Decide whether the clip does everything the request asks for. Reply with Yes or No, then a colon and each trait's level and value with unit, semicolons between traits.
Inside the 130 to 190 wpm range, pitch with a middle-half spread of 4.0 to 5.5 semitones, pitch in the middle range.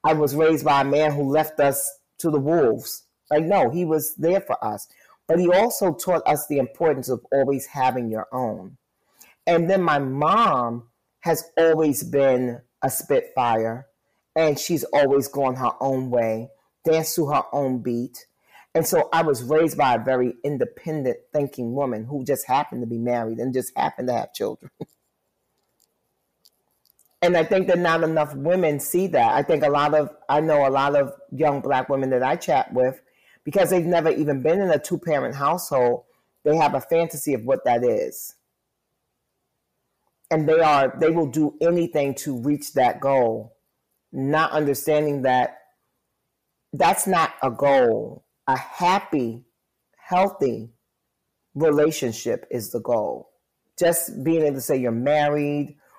No: average, 160 wpm; average, 3.6 semitones; medium, 145 Hz